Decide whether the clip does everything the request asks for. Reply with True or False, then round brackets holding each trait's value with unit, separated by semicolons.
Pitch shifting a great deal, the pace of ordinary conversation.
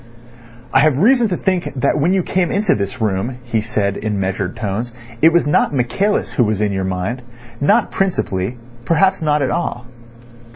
True (8.4 semitones; 175 wpm)